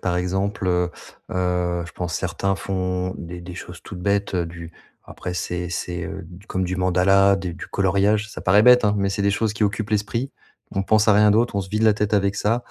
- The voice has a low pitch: Yes, very low, 95 Hz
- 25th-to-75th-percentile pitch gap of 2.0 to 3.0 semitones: Yes, narrow, 2.5 semitones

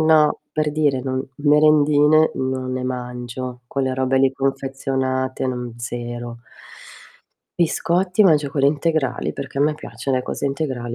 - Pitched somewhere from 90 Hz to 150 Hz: Yes, low, 135 Hz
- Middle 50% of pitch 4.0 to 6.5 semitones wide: No, average, 2.7 semitones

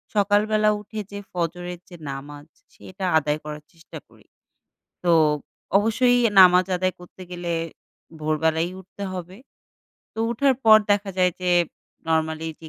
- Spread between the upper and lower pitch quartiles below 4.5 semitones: Yes, average, 4.1 semitones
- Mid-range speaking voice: Yes, medium, 180 Hz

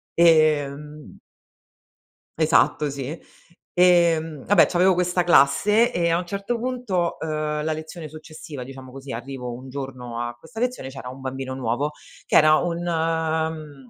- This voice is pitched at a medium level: Yes, medium, 155 Hz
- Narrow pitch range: No, average, 4.3 semitones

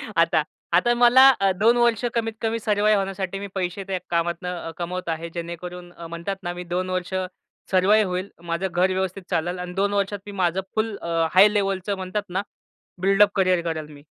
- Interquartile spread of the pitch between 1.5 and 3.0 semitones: Yes, narrow, 2.6 semitones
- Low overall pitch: No, medium, 185 Hz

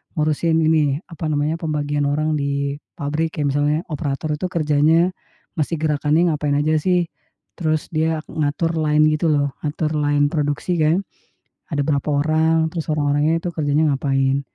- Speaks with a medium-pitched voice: Yes, medium, 150 Hz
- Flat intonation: Yes, narrow, 1.7 semitones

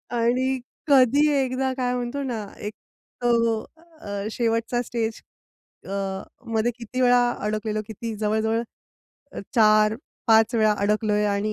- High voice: Yes, high, 230 Hz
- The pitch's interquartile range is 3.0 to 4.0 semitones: No, narrow, 2.4 semitones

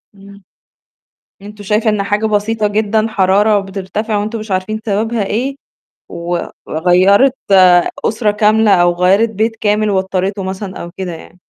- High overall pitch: Yes, high, 205 Hz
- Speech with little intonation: Yes, narrow, 2.3 semitones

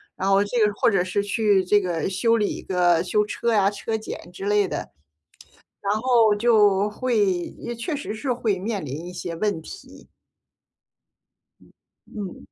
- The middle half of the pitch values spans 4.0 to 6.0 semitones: No, average, 3.2 semitones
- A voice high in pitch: Yes, high, 205 Hz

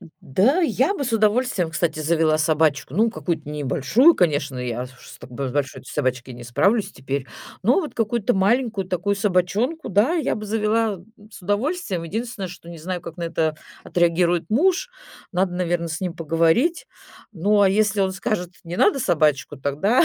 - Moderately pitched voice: Yes, medium, 180 Hz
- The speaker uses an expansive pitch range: Yes, wide, 5.7 semitones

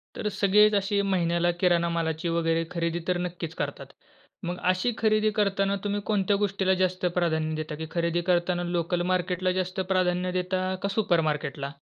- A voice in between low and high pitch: Yes, medium, 180 Hz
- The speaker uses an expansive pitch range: No, narrow, 2.5 semitones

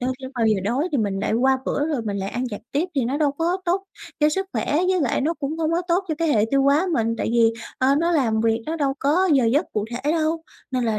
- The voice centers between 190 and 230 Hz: No, very high, 275 Hz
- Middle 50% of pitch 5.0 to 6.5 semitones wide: Yes, wide, 5.6 semitones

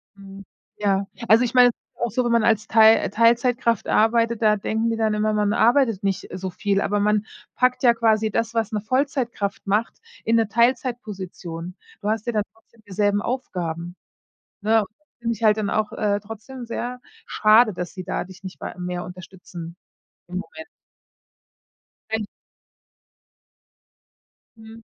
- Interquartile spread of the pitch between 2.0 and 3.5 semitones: Yes, average, 2.7 semitones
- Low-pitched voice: No, high, 215 Hz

